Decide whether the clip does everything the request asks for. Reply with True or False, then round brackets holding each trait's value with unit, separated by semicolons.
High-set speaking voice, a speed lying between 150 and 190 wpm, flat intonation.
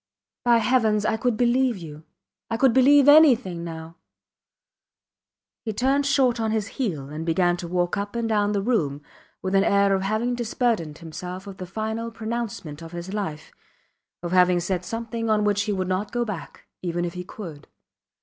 False (205 Hz; 180 wpm; 4.8 semitones)